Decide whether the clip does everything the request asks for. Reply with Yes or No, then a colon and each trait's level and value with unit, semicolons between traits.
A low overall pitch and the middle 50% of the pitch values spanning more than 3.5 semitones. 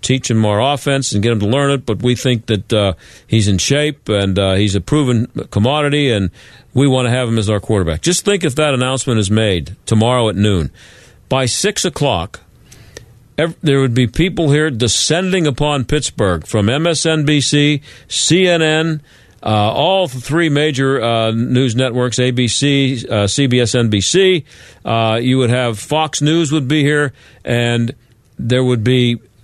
Yes: low, 125 Hz; average, 4.7 semitones